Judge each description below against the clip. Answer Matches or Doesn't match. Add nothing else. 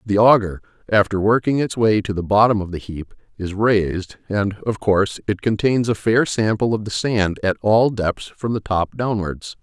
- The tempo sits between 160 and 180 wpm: Doesn't match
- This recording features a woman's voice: Doesn't match